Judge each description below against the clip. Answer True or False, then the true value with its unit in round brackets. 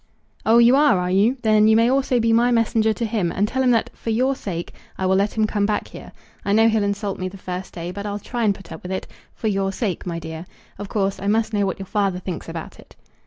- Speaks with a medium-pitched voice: False (205 Hz)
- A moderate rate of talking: False (270 wpm)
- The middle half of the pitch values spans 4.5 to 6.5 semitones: False (3.2 semitones)